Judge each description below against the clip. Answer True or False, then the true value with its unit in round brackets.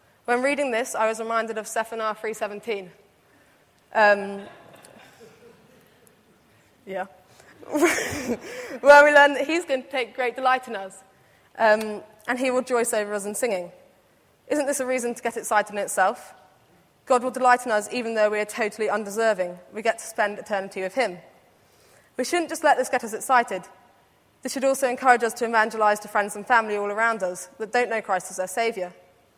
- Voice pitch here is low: False (225 Hz)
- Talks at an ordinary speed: True (180 wpm)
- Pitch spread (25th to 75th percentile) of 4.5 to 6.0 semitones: False (3.6 semitones)